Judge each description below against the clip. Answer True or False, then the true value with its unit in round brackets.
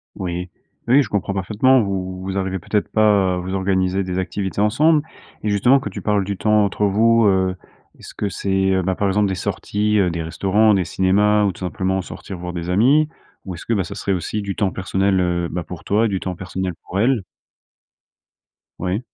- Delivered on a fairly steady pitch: True (2.2 semitones)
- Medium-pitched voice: False (95 Hz)